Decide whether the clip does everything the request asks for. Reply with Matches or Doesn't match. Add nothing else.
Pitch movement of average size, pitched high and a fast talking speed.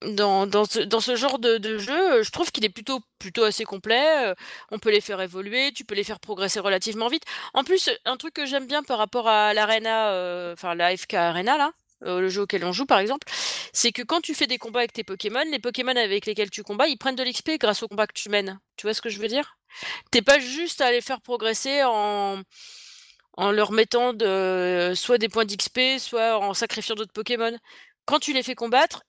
Matches